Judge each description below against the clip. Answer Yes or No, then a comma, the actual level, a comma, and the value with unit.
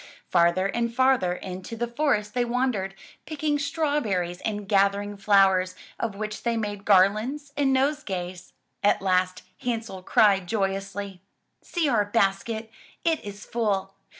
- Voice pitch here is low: No, high, 205 Hz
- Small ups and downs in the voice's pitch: No, average, 3.7 semitones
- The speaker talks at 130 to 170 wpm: Yes, slow, 135 wpm